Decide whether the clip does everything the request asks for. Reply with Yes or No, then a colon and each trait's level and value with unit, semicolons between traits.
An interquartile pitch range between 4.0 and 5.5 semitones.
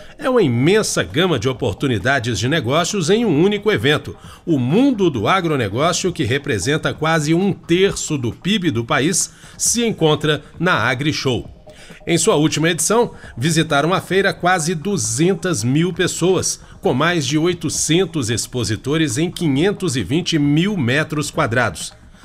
Yes: average, 4.4 semitones